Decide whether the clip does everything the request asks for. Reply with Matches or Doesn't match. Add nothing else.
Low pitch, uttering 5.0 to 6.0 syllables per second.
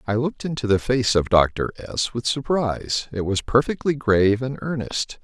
Doesn't match